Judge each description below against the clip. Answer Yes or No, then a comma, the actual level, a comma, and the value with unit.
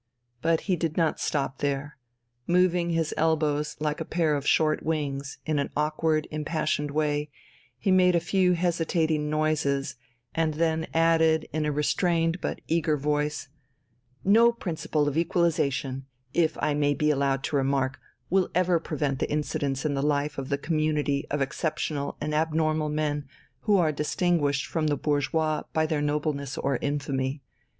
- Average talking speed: Yes, average, 160 wpm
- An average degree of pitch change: No, narrow, 2.1 semitones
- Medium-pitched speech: Yes, medium, 150 Hz